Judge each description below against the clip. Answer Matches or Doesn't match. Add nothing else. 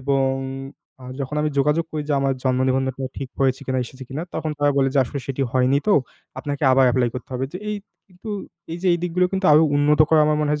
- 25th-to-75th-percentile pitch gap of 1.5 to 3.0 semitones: Matches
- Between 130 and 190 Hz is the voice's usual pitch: Matches